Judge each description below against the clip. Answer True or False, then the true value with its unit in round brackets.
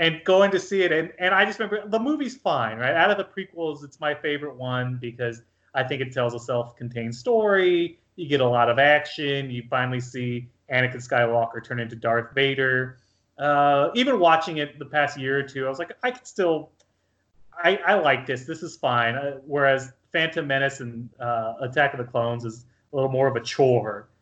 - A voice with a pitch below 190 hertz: True (135 Hz)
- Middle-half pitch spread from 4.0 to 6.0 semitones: True (5.2 semitones)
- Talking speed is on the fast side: True (210 wpm)